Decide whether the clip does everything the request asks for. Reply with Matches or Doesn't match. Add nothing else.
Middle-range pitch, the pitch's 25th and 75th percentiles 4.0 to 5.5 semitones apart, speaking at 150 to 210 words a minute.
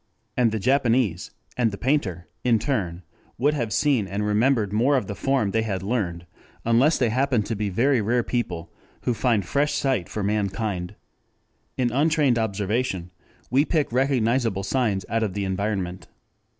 Doesn't match